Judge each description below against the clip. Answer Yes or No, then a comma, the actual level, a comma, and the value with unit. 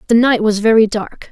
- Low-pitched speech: No, high, 220 Hz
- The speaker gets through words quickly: Yes, fast, 225 wpm